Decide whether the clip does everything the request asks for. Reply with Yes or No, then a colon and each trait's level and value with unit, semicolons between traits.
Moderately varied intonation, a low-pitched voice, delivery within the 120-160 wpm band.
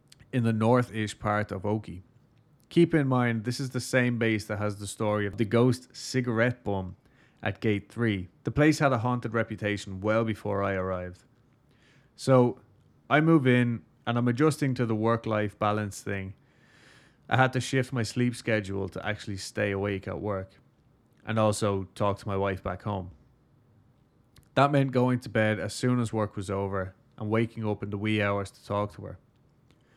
No: average, 3.5 semitones; low, 115 Hz; average, 185 wpm